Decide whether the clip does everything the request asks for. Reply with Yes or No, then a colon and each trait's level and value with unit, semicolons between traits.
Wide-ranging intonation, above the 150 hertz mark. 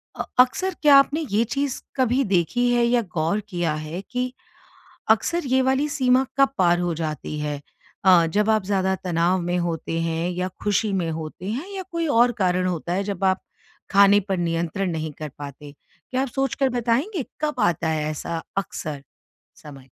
Yes: wide, 7.2 semitones; high, 190 Hz